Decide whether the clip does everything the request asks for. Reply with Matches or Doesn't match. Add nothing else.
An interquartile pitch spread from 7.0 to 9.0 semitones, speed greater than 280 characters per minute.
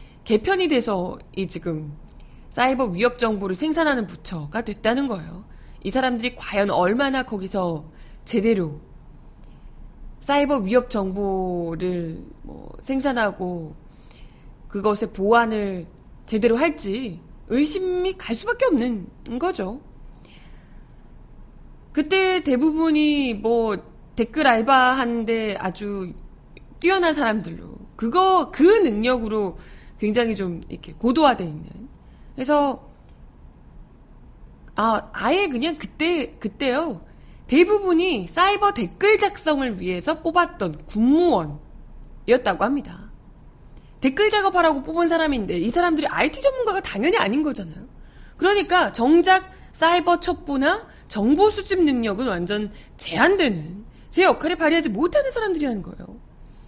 Doesn't match